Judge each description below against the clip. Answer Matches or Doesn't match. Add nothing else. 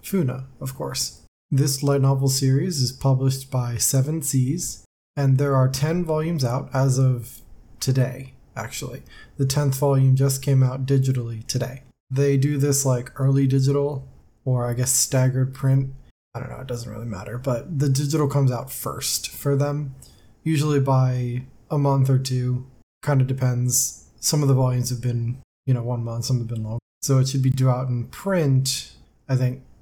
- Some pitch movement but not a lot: Doesn't match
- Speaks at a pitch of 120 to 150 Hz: Matches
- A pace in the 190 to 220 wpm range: Doesn't match